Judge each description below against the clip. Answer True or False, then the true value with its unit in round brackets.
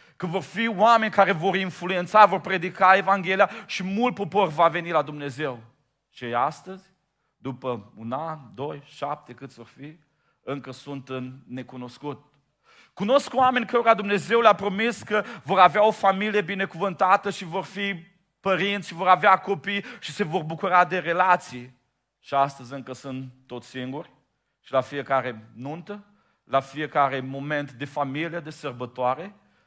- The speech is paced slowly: False (150 wpm)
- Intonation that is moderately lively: False (6.3 semitones)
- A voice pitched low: False (170 Hz)